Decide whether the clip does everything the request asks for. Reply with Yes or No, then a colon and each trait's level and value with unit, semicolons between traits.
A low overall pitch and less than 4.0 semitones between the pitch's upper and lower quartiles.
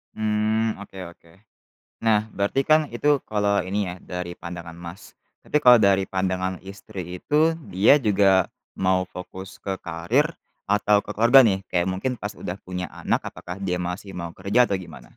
Yes: very low, 95 Hz; average, 2.8 semitones